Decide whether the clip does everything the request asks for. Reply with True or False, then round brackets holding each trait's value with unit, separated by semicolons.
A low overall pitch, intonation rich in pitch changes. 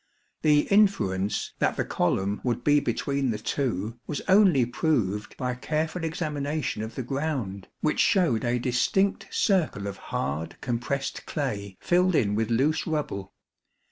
True (130 Hz; 6.6 semitones)